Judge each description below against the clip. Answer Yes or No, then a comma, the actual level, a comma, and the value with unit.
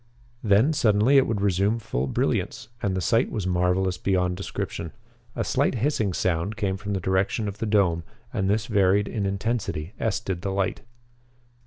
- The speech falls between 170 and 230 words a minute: Yes, average, 175 wpm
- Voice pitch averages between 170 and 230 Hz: No, low, 100 Hz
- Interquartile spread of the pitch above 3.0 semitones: No, average, 2.7 semitones